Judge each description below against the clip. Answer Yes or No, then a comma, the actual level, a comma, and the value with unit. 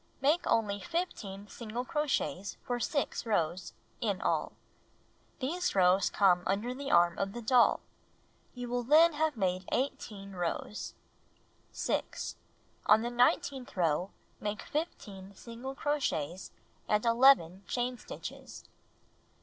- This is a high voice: Yes, high, 230 Hz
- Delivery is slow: Yes, slow, 125 wpm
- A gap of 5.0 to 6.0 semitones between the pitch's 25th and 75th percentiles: Yes, wide, 5.5 semitones